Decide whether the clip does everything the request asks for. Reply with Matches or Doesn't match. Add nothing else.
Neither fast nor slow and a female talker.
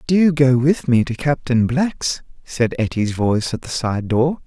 Doesn't match